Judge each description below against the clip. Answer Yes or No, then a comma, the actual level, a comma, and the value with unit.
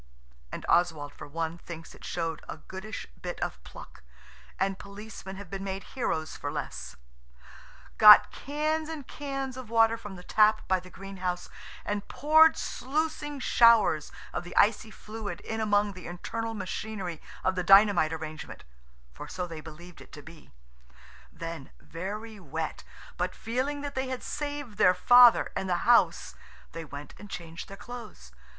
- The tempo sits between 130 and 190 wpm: Yes, average, 155 wpm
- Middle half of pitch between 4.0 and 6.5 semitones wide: Yes, wide, 5.5 semitones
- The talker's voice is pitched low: No, high, 195 Hz